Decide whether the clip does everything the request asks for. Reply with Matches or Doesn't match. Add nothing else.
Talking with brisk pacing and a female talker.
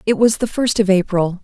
Matches